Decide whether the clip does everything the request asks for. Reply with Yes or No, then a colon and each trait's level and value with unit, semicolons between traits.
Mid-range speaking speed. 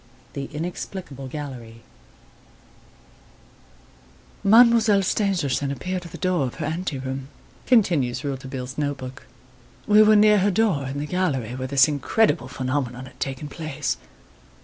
No: slow, 130 wpm